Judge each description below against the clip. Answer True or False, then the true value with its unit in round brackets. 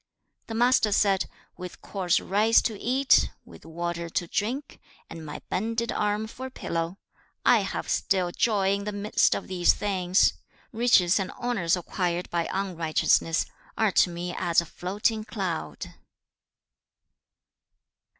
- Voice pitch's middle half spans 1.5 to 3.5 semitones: False (3.9 semitones)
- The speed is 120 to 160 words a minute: True (140 wpm)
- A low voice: False (195 Hz)